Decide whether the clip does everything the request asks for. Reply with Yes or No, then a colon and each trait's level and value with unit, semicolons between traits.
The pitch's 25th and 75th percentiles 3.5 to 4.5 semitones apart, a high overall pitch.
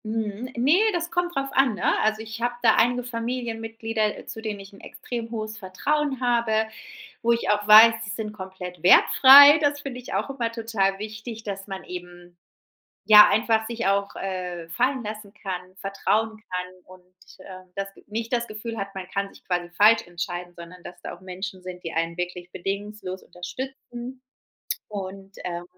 Yes: average, 3.8 semitones; high, 215 Hz